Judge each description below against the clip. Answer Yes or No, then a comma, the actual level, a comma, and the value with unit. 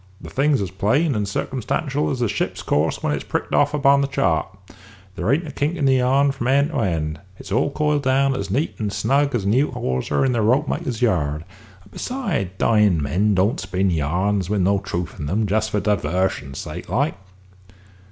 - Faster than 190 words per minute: Yes, average, 200 wpm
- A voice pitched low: Yes, low, 110 Hz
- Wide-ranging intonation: Yes, wide, 6.8 semitones